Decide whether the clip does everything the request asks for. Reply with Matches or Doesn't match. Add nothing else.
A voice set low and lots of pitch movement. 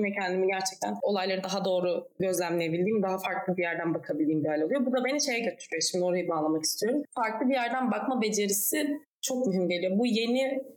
Doesn't match